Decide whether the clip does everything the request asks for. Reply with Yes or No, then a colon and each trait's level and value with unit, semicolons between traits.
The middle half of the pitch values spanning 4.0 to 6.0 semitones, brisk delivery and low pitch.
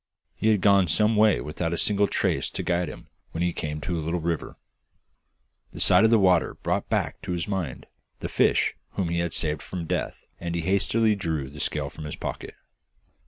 No: average, 3.6 semitones; fast, 210 wpm; very low, 85 Hz